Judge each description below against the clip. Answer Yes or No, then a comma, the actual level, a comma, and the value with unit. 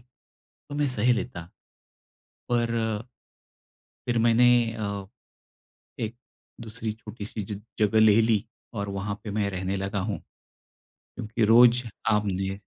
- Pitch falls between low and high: No, low, 110 Hz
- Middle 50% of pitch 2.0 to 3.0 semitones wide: Yes, narrow, 2.5 semitones